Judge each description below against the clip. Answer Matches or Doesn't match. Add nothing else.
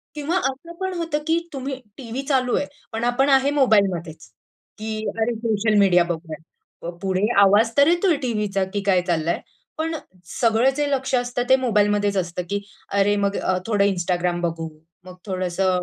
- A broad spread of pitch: Matches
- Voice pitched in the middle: Doesn't match